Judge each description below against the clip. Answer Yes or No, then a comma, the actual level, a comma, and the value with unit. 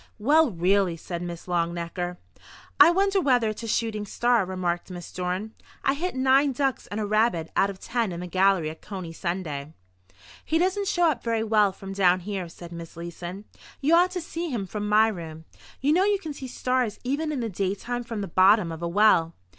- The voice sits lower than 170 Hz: No, high, 205 Hz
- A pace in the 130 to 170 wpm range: No, fast, 205 wpm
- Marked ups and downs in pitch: Yes, wide, 6.4 semitones